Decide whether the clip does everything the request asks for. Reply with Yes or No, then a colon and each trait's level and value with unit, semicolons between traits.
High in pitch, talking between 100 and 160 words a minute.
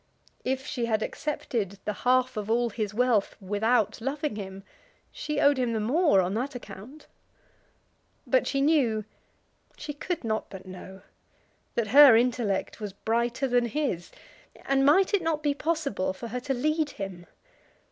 Yes: high, 240 Hz; average, 155 wpm